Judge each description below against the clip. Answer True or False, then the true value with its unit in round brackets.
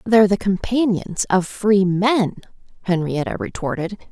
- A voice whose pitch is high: True (195 Hz)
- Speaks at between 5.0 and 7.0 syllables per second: False (4.5 syllables/s)